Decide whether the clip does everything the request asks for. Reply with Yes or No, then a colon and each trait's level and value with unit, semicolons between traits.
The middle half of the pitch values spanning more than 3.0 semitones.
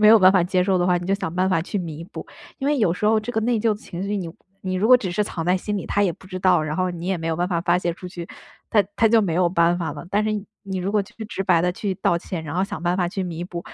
No: narrow, 2.6 semitones